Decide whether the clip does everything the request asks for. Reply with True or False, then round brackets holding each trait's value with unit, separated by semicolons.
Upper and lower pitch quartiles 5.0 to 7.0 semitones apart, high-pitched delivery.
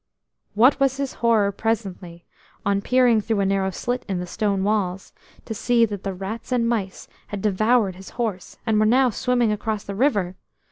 False (3.4 semitones; 215 Hz)